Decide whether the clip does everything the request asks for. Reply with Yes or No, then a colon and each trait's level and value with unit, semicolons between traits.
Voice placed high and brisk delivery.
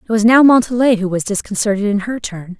Yes: high, 215 Hz; fast, 230 wpm